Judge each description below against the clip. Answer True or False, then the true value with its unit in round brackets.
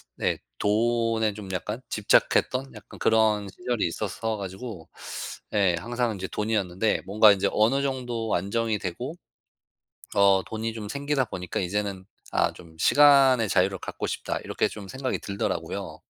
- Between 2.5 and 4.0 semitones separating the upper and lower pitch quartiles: True (3.4 semitones)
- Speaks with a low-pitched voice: True (110 Hz)